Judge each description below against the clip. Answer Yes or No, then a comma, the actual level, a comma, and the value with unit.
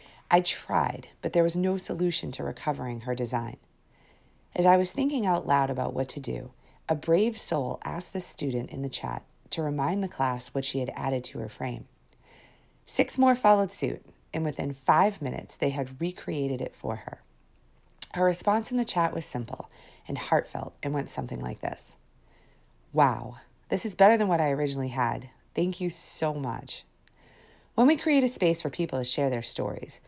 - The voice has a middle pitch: Yes, medium, 155 Hz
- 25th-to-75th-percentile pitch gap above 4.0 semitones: Yes, wide, 5.6 semitones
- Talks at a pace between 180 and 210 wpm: Yes, average, 185 wpm